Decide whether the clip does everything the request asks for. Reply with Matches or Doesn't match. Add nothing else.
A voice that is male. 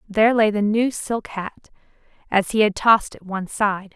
Doesn't match